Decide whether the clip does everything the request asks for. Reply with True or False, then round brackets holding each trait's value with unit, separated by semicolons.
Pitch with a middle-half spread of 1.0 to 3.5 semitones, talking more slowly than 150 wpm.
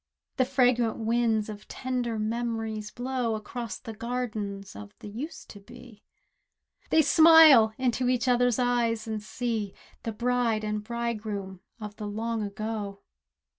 True (2.5 semitones; 135 wpm)